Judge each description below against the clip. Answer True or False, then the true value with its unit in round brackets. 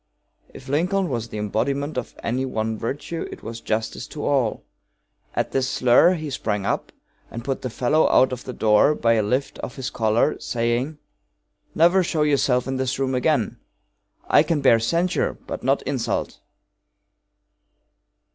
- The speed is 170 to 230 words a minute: False (160 wpm)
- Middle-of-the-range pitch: False (130 Hz)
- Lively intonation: False (4.1 semitones)